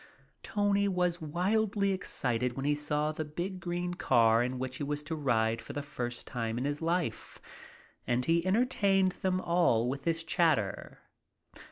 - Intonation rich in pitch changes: Yes, wide, 6.2 semitones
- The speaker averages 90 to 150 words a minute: No, average, 170 wpm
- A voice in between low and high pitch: Yes, medium, 155 Hz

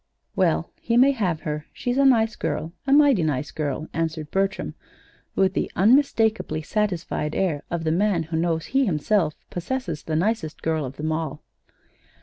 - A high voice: No, medium, 170 Hz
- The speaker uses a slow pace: No, average, 165 wpm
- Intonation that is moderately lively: No, wide, 6.0 semitones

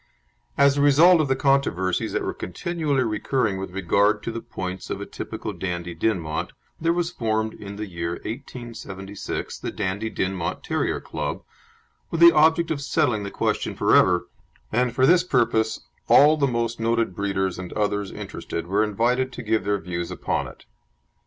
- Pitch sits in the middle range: No, low, 110 Hz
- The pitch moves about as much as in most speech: No, wide, 6.1 semitones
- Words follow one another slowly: No, average, 170 wpm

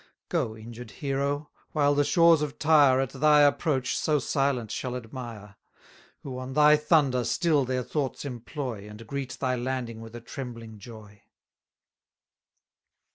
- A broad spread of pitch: No, average, 3.6 semitones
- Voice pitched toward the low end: Yes, low, 130 Hz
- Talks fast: No, average, 140 wpm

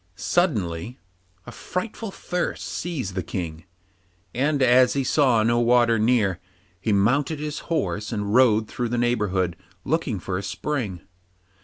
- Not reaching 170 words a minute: Yes, average, 140 wpm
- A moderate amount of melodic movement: No, wide, 5.7 semitones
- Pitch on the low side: Yes, low, 120 Hz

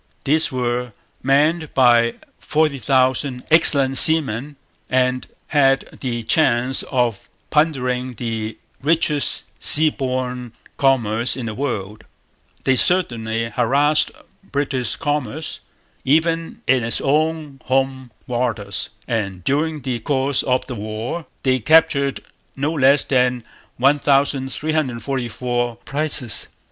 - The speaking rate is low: Yes, slow, 105 wpm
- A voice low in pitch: Yes, low, 130 Hz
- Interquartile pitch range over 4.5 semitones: No, average, 3.3 semitones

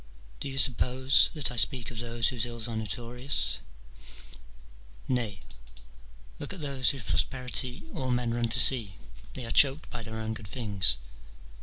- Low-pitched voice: Yes, low, 120 Hz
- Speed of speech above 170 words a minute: No, average, 160 wpm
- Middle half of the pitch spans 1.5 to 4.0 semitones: Yes, average, 2.7 semitones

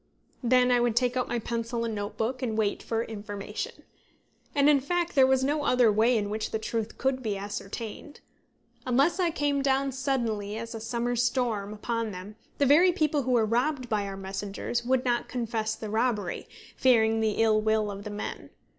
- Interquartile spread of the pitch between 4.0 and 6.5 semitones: No, average, 3.3 semitones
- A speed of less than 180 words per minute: No, average, 190 wpm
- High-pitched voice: Yes, high, 235 Hz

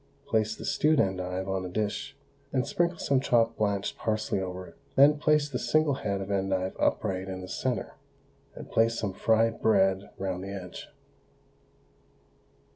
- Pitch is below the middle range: Yes, low, 100 Hz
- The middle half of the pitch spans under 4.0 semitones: Yes, average, 3.6 semitones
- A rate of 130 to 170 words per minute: Yes, average, 160 wpm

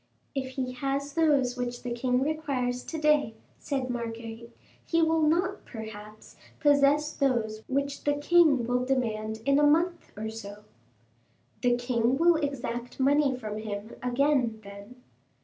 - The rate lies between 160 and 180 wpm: No, average, 145 wpm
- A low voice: No, very high, 255 Hz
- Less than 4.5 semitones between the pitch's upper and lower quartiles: Yes, average, 3.9 semitones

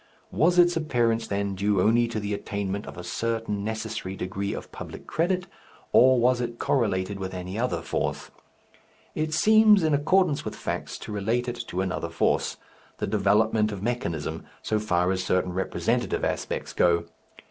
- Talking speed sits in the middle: Yes, average, 165 wpm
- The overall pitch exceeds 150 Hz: No, low, 105 Hz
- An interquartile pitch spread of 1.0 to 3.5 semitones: No, average, 4.4 semitones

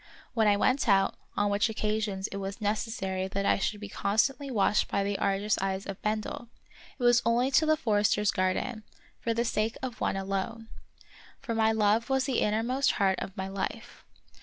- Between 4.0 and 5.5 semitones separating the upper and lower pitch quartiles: No, average, 2.8 semitones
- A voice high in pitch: Yes, high, 210 Hz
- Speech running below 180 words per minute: No, average, 185 wpm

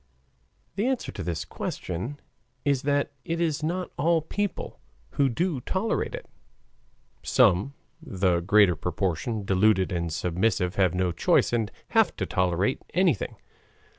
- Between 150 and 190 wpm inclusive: No, slow, 135 wpm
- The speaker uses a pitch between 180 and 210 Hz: No, low, 110 Hz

